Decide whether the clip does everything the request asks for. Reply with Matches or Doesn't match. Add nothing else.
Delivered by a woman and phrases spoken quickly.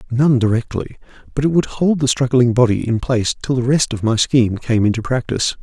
Doesn't match